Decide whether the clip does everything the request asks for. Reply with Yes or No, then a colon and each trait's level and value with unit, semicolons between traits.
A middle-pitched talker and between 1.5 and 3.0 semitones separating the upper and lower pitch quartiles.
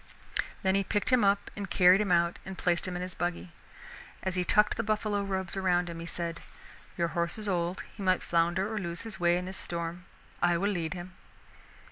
Yes: medium, 180 Hz; narrow, 2.4 semitones